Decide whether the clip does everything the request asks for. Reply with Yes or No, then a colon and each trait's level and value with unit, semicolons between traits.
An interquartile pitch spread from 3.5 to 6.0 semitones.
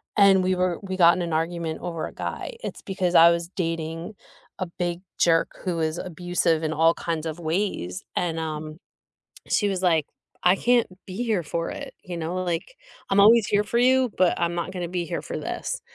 No: narrow, 2.4 semitones